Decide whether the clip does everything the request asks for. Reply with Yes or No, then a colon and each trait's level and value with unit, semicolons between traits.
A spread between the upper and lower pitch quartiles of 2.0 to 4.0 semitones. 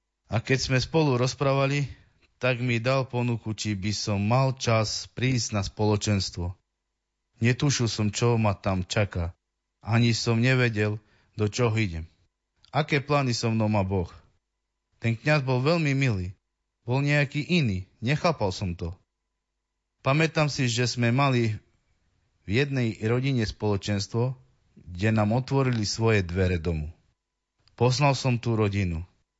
No: average, 5.0 semitones